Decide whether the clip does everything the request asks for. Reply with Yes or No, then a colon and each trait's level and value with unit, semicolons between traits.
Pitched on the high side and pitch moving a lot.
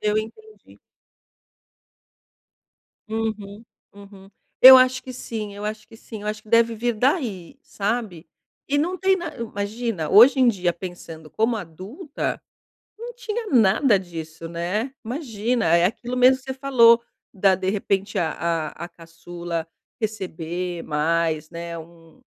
Yes: high, 210 Hz; wide, 5.8 semitones